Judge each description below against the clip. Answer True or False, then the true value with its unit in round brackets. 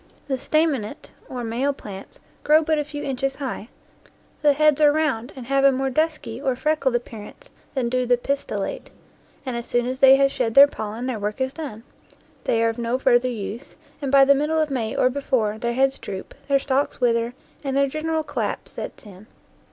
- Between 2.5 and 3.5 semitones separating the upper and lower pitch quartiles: True (3.0 semitones)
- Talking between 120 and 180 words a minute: False (205 wpm)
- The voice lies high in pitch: True (265 Hz)